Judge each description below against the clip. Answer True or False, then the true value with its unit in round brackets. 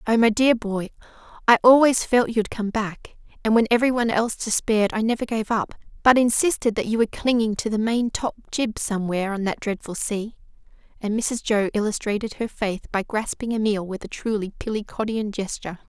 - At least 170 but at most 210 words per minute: True (185 wpm)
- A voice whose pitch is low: False (220 Hz)